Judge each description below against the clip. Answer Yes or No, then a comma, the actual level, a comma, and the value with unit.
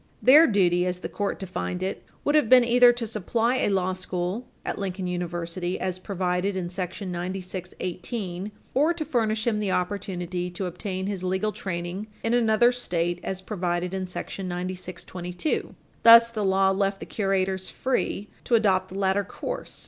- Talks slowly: No, average, 165 wpm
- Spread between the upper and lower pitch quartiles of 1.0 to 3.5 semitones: Yes, average, 3.2 semitones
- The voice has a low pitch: No, high, 190 Hz